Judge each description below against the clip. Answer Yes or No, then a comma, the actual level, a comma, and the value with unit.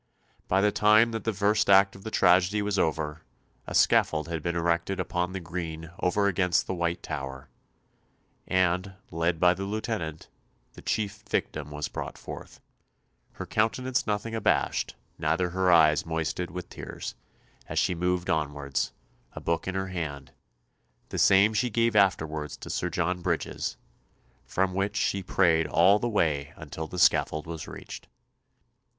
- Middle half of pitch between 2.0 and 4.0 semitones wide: Yes, average, 3.7 semitones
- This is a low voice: Yes, very low, 90 Hz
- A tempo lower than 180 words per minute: Yes, average, 155 wpm